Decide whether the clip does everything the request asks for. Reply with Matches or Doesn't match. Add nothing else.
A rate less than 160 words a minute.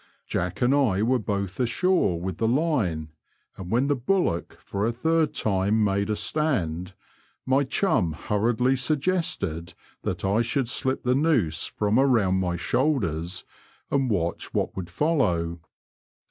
Matches